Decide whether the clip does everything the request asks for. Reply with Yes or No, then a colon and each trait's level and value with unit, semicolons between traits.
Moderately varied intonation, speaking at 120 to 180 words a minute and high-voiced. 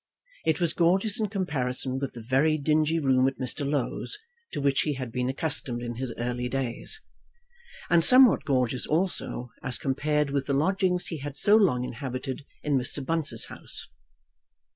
No: average, 4.2 semitones; average, 165 wpm; medium, 140 Hz